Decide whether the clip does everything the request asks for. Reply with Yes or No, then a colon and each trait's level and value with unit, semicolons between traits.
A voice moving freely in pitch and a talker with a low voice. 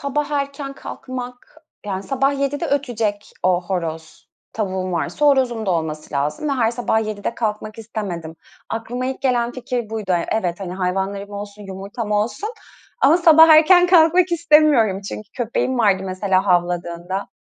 No: wide, 6.3 semitones; high, 220 Hz